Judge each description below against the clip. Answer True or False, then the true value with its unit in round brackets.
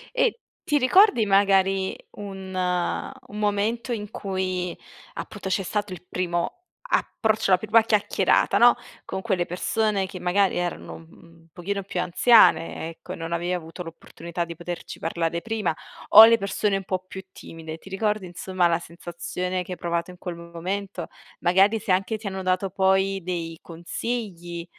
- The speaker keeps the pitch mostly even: False (3.0 semitones)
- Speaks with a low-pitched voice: False (185 Hz)